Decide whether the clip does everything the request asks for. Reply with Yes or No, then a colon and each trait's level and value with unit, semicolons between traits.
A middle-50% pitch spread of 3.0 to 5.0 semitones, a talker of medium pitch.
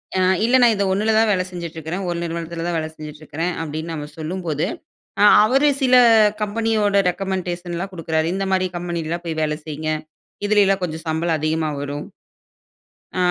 Yes: average, 3.5 semitones; medium, 170 Hz